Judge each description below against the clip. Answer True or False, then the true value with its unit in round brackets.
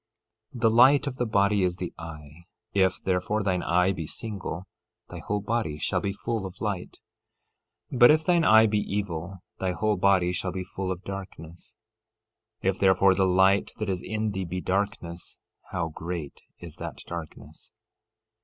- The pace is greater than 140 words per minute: True (170 wpm)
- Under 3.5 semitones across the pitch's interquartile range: True (2.8 semitones)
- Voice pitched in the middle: False (95 Hz)